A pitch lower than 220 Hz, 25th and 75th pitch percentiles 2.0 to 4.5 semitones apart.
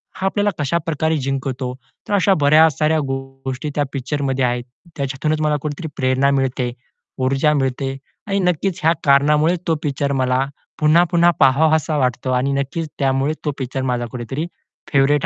Yes: medium, 140 Hz; average, 2.9 semitones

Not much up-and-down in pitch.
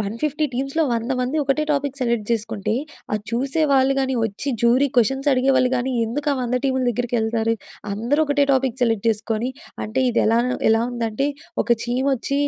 No: average, 3.0 semitones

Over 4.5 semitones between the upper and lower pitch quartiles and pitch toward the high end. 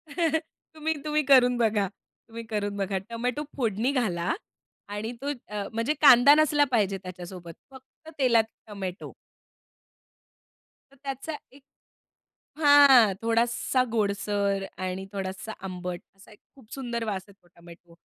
Yes: average, 5.3 semitones; high, 225 Hz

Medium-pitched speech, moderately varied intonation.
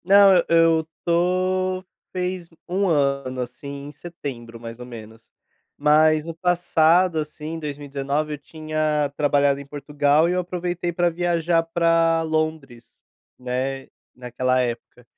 Yes: medium, 155 Hz; average, 3.8 semitones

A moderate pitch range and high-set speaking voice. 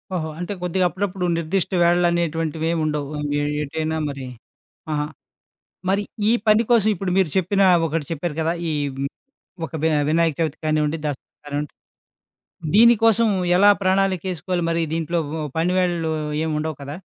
No: average, 3.2 semitones; medium, 165 Hz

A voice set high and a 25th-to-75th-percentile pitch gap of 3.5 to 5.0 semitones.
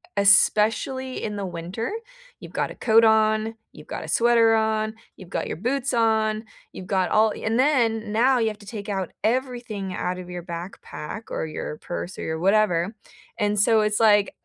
No: high, 215 Hz; average, 2.8 semitones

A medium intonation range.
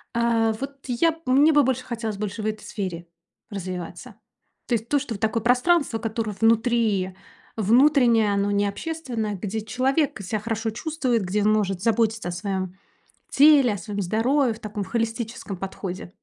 Yes: average, 3.4 semitones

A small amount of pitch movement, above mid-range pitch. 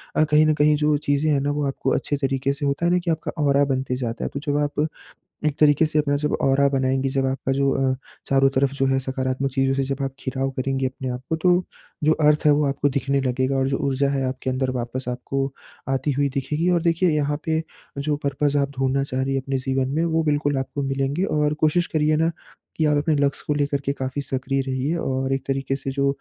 No: narrow, 1.9 semitones; medium, 140 Hz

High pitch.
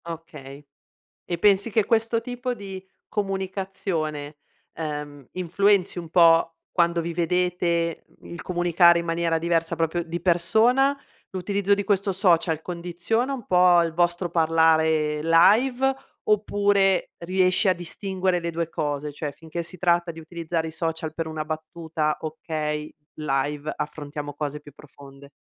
No: medium, 170 Hz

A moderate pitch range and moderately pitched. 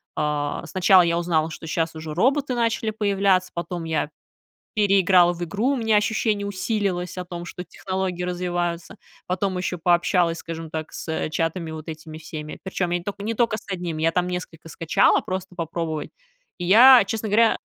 Yes: average, 3.4 semitones; medium, 180 Hz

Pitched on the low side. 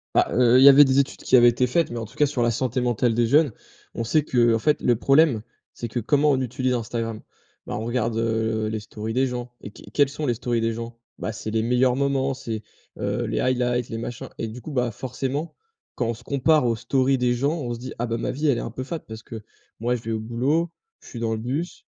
Yes: low, 120 Hz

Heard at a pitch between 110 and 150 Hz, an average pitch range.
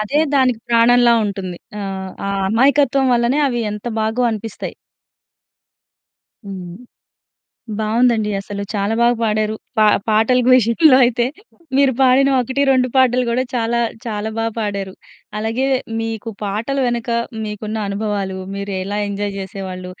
No: high, 225 Hz; average, 3.3 semitones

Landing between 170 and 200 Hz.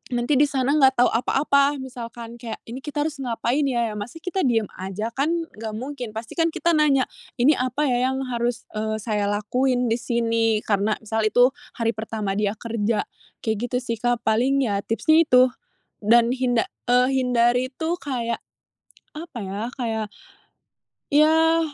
No: high, 245 Hz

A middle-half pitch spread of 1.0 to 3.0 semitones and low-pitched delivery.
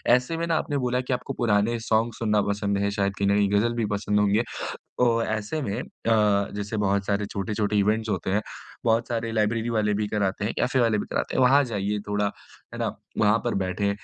Yes: narrow, 2.4 semitones; low, 105 Hz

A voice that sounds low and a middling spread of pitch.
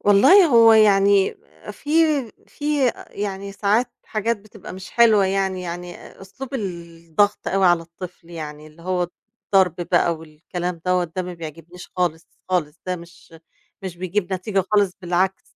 No: medium, 185 Hz; average, 3.2 semitones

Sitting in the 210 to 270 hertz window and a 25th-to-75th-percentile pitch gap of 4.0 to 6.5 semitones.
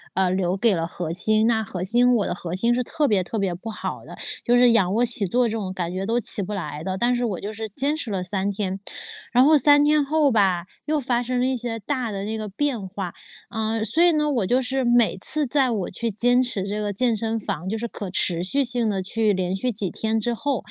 Yes: high, 220 Hz; average, 4.3 semitones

